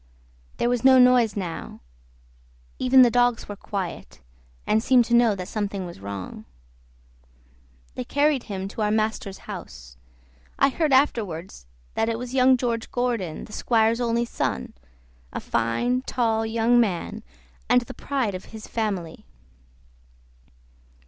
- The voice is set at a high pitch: Yes, high, 225 Hz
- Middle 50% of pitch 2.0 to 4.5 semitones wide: Yes, average, 3.9 semitones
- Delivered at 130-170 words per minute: Yes, average, 140 wpm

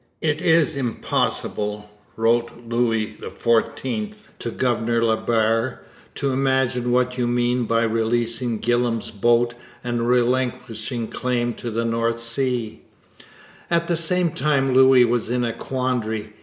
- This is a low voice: Yes, low, 120 Hz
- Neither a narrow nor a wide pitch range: No, narrow, 1.9 semitones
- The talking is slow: Yes, slow, 130 wpm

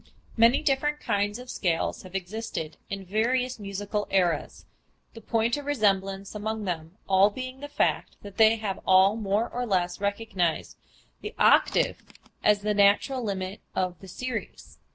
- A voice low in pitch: No, high, 205 Hz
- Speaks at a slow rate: No, average, 155 wpm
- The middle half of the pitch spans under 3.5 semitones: Yes, average, 3.1 semitones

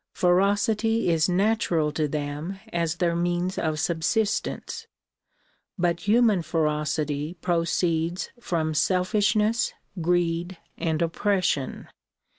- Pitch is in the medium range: Yes, medium, 175 Hz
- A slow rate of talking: Yes, slow, 90 wpm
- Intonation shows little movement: No, average, 3.5 semitones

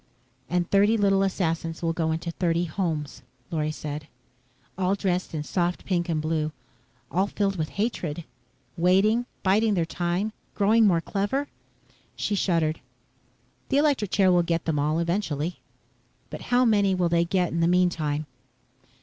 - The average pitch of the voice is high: No, medium, 175 Hz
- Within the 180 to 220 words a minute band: No, average, 150 wpm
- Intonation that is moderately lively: Yes, average, 3.3 semitones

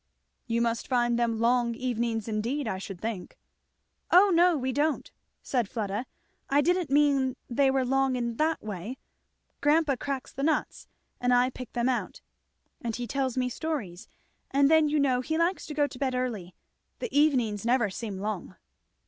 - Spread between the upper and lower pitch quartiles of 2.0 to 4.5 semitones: Yes, average, 3.8 semitones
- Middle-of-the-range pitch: No, very high, 255 Hz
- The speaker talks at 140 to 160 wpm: No, average, 175 wpm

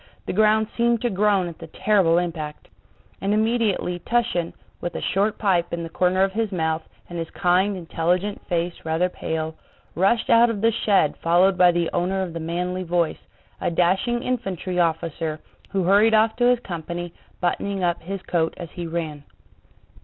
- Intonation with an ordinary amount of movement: Yes, average, 3.4 semitones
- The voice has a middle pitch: Yes, medium, 180 Hz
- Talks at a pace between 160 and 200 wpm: Yes, average, 175 wpm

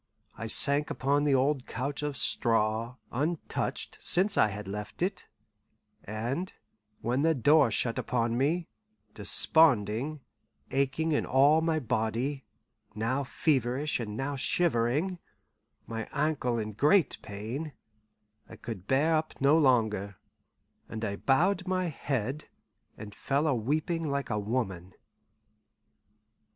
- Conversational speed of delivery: No, slow, 125 wpm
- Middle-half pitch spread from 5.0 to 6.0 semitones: Yes, average, 5.3 semitones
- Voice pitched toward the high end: No, low, 135 Hz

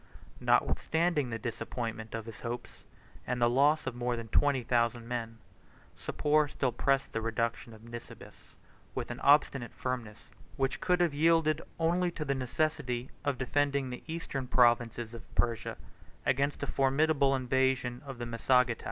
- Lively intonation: No, average, 3.4 semitones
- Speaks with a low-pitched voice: Yes, low, 125 Hz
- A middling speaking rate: Yes, average, 150 wpm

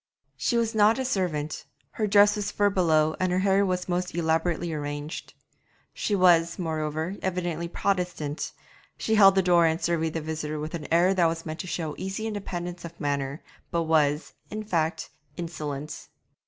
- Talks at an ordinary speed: Yes, average, 170 wpm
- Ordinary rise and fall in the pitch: Yes, average, 3.3 semitones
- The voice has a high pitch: No, medium, 170 Hz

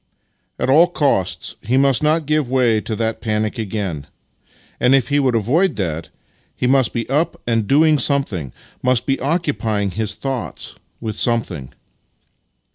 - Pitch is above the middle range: No, low, 125 Hz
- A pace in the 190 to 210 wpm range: No, average, 155 wpm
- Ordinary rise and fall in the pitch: Yes, average, 4.6 semitones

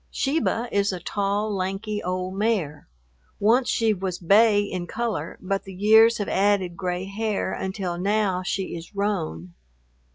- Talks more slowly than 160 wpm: Yes, average, 150 wpm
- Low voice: No, high, 200 Hz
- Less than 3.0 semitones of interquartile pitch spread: Yes, narrow, 2.6 semitones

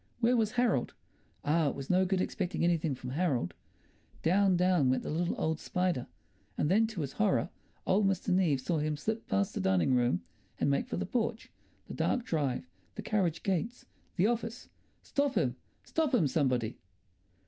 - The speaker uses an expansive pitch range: Yes, wide, 7.3 semitones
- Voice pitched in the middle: Yes, medium, 175 Hz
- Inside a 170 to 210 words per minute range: Yes, average, 180 wpm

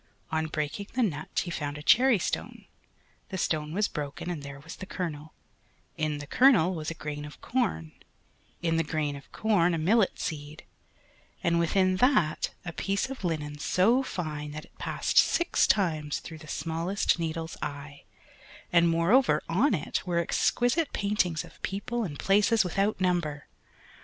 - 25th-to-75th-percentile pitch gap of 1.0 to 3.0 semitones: No, average, 4.6 semitones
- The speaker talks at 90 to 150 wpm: No, average, 165 wpm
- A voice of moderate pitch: Yes, medium, 170 Hz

